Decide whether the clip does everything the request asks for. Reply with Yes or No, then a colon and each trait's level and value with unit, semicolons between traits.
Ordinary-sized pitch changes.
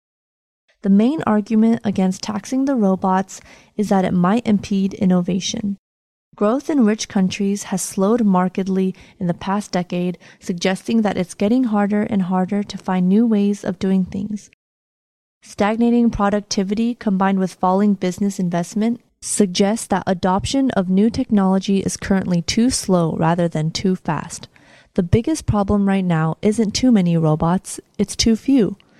No: narrow, 2.3 semitones